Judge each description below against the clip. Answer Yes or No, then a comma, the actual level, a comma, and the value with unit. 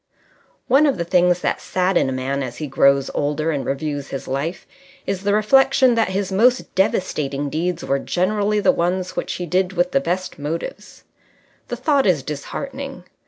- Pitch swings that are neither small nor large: No, wide, 5.8 semitones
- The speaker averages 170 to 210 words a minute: Yes, average, 180 wpm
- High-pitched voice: No, medium, 180 Hz